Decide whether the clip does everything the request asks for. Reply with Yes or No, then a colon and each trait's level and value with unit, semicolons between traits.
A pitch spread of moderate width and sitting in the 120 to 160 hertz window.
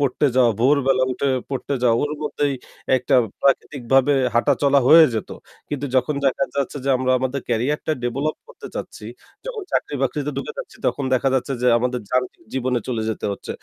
No: narrow, 2.3 semitones; low, 135 Hz